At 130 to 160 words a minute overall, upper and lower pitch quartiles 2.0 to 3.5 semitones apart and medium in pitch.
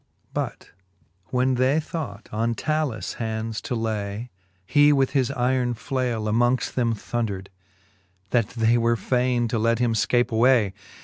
No: average, 145 wpm; narrow, 2.4 semitones; low, 120 Hz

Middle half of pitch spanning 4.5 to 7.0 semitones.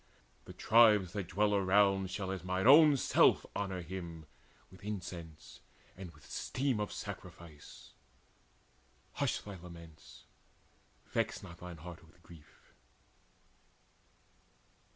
No: average, 3.3 semitones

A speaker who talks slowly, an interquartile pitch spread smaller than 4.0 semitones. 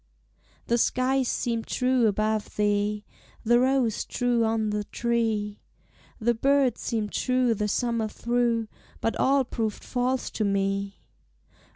Yes: slow, 130 wpm; average, 2.8 semitones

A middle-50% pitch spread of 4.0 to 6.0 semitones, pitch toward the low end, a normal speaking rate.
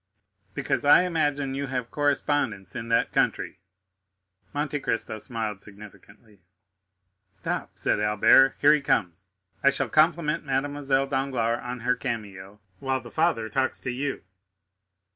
No: average, 4.6 semitones; low, 130 Hz; slow, 130 wpm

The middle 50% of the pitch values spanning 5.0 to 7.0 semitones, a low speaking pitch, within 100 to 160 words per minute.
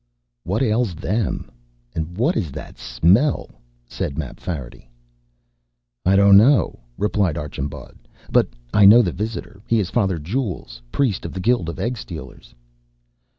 Yes: wide, 5.6 semitones; low, 100 Hz; slow, 135 wpm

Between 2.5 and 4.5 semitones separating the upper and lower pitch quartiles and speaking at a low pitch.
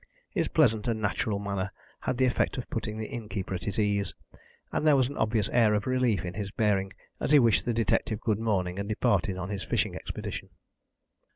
Yes: average, 3.0 semitones; low, 105 Hz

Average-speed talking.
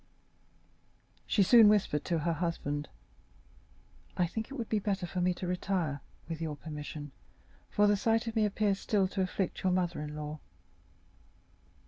Yes: average, 160 wpm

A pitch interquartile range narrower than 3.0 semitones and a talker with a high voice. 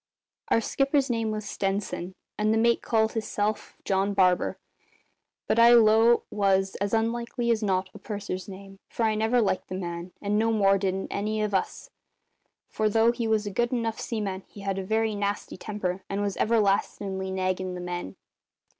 Yes: narrow, 2.6 semitones; high, 205 Hz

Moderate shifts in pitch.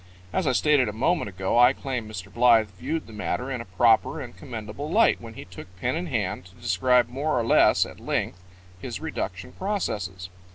No: wide, 5.8 semitones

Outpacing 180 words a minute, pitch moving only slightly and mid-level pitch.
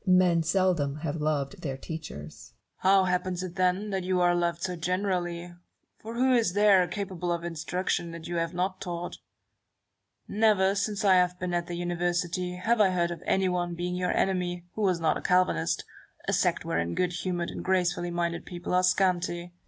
Yes: average, 200 wpm; narrow, 1.4 semitones; medium, 180 Hz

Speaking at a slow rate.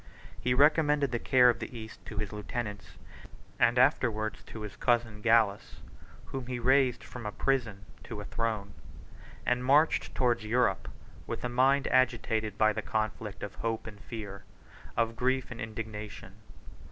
No: average, 155 wpm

